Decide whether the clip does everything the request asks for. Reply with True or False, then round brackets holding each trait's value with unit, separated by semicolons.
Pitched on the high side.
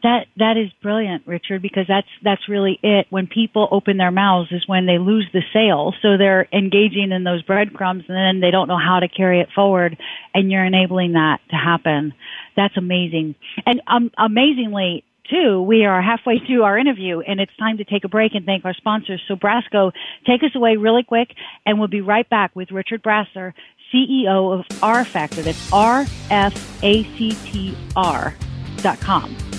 True (200 Hz)